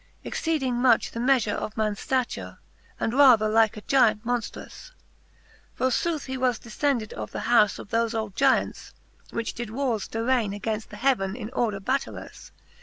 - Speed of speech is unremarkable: Yes, average, 165 wpm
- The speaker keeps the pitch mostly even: No, average, 3.2 semitones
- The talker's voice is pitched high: Yes, high, 230 Hz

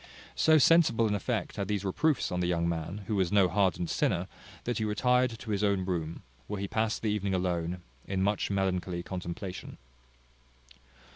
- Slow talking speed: No, average, 180 wpm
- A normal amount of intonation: Yes, average, 3.0 semitones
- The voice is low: Yes, low, 100 Hz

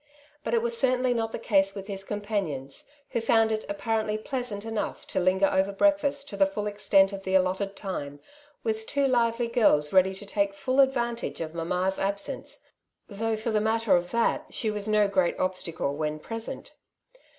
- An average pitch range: Yes, average, 3.2 semitones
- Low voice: No, high, 210 Hz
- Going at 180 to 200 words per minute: Yes, average, 190 wpm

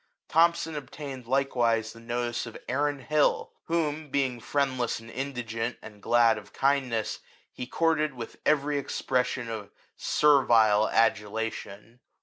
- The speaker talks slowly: Yes, slow, 130 wpm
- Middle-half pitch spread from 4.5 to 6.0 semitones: No, average, 3.9 semitones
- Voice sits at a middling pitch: No, low, 125 Hz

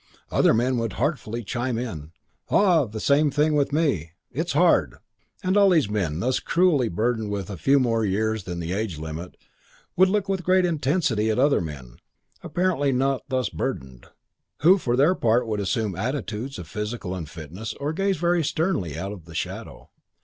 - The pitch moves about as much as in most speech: No, wide, 7.2 semitones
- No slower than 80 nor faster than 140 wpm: No, average, 175 wpm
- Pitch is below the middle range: Yes, low, 120 Hz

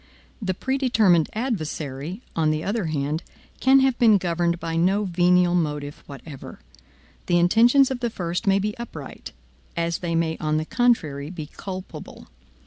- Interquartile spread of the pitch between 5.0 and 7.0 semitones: Yes, wide, 5.4 semitones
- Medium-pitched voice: Yes, medium, 175 Hz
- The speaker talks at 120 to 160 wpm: Yes, average, 150 wpm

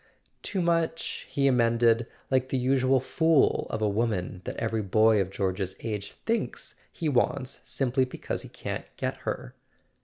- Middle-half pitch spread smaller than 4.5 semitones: Yes, average, 4.0 semitones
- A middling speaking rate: Yes, average, 155 wpm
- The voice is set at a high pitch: No, low, 120 Hz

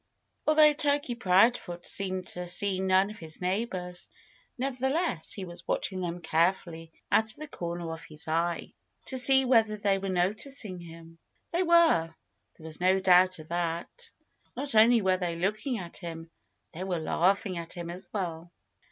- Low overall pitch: No, medium, 185 Hz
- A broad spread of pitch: No, average, 4.6 semitones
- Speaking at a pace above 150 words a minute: Yes, average, 165 wpm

